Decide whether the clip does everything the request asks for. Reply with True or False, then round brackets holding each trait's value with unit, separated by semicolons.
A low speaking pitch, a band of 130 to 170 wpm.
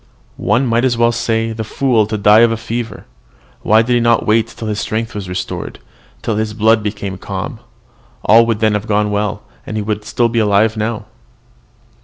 False (110 Hz; 200 wpm)